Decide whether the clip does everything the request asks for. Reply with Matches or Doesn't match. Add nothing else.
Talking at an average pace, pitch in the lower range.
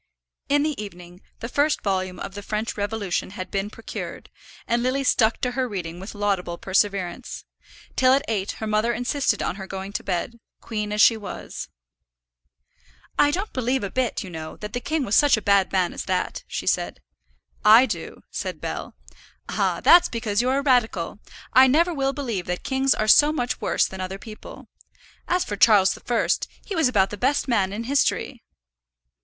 Doesn't match